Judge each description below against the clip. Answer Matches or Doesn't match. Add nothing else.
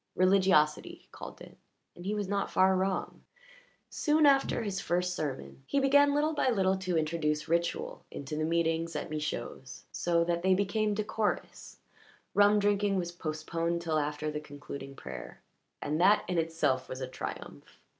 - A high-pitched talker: Doesn't match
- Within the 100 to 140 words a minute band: Doesn't match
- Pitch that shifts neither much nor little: Matches